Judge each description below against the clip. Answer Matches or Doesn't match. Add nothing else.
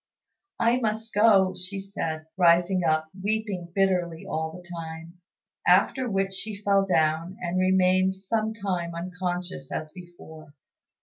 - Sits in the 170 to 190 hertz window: Matches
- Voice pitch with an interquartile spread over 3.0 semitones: Doesn't match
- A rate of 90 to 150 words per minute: Matches